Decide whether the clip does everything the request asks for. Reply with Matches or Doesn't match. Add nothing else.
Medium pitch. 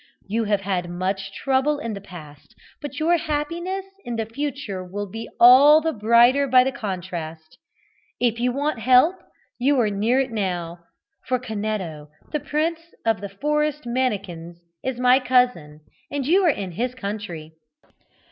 Doesn't match